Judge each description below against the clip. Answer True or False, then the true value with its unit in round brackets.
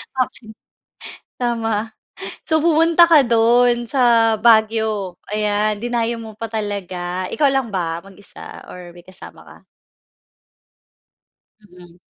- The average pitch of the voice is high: True (225 Hz)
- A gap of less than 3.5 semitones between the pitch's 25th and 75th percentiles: True (3.1 semitones)